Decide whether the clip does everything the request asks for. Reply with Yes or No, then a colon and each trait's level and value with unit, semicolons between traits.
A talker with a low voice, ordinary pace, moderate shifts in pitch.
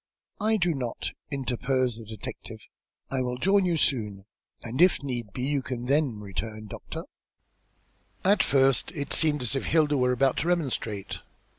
Yes: low, 130 Hz; average, 160 wpm; average, 4.0 semitones